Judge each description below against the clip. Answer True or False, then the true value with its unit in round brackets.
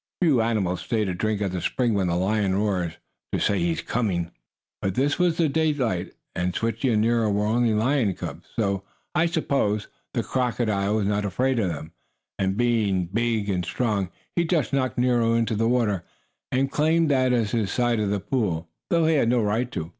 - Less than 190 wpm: False (200 wpm)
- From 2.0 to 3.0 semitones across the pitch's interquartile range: False (4.2 semitones)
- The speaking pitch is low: True (110 Hz)